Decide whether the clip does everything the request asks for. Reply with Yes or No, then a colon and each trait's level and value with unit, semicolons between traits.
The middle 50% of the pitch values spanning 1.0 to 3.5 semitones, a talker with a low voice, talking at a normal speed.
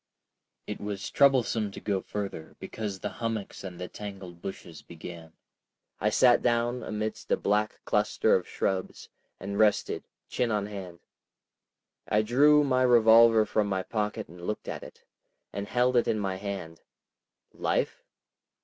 Yes: average, 3.1 semitones; low, 105 Hz; average, 150 wpm